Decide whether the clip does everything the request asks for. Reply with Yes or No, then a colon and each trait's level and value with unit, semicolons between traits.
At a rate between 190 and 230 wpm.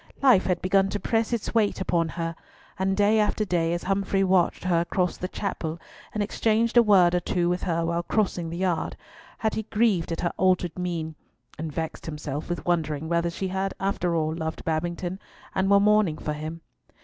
Yes: average, 195 wpm